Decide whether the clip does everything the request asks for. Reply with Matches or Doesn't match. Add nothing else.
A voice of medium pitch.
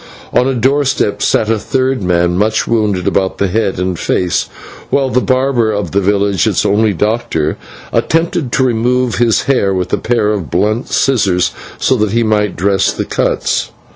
Doesn't match